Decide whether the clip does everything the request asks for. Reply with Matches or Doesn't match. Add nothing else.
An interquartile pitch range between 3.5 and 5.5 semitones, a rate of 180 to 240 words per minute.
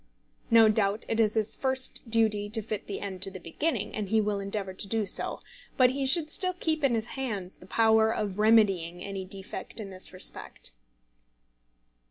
Doesn't match